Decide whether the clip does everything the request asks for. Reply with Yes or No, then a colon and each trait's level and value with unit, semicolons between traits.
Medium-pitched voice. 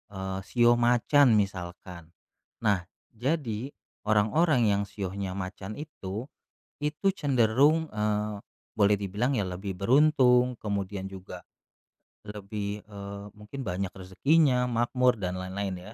No: low, 105 Hz